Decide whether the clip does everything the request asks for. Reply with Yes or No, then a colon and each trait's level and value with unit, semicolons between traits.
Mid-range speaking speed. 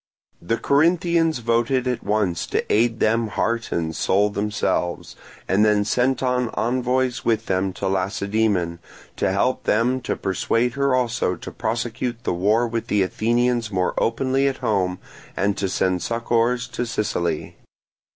Yes: average, 150 wpm